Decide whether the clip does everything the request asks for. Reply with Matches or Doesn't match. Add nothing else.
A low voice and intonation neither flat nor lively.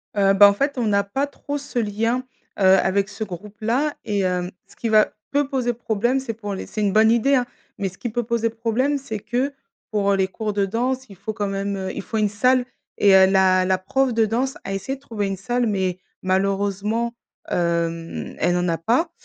Doesn't match